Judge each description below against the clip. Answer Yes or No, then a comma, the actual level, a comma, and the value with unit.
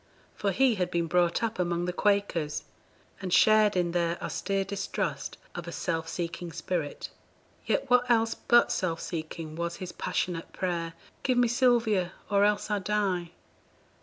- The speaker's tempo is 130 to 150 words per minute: No, average, 160 wpm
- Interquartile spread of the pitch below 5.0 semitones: Yes, average, 3.6 semitones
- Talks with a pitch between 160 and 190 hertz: Yes, medium, 185 Hz